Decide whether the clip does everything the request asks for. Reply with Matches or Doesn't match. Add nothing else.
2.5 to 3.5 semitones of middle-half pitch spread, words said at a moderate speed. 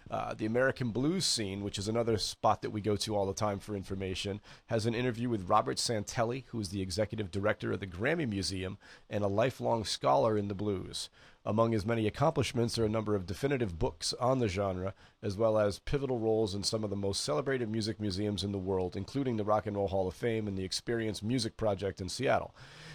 Doesn't match